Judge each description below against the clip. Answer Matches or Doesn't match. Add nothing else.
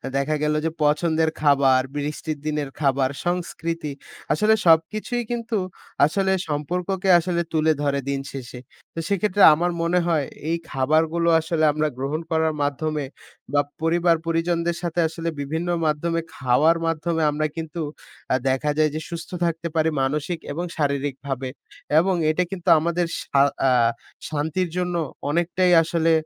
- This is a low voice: Doesn't match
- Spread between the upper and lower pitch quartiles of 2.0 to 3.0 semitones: Matches